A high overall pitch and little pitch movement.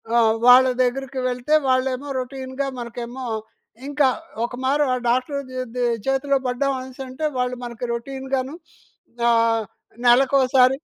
Yes: very high, 255 Hz; narrow, 1.5 semitones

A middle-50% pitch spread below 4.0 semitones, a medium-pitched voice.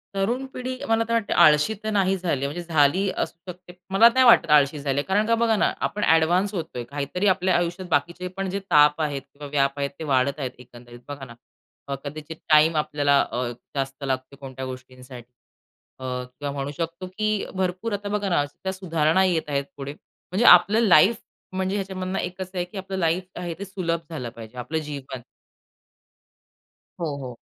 No: average, 5.2 semitones; medium, 165 Hz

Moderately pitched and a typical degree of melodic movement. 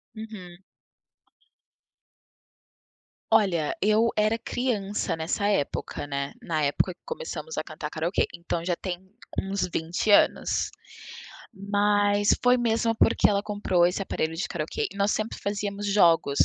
No: high, 200 Hz; average, 3.6 semitones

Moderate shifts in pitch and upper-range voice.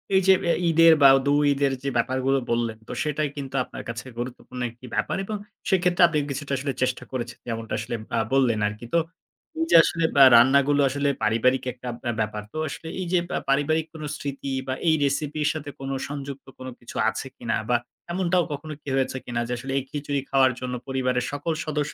No: average, 3.1 semitones; low, 135 Hz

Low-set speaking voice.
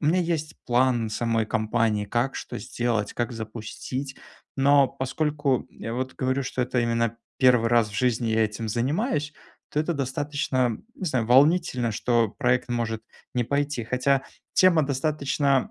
Yes: low, 125 Hz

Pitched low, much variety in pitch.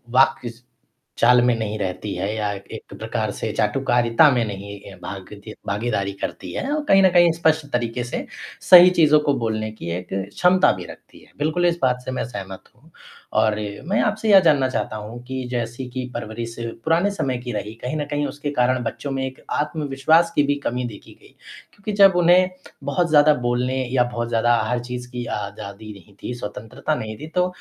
Yes: low, 125 Hz; wide, 6.0 semitones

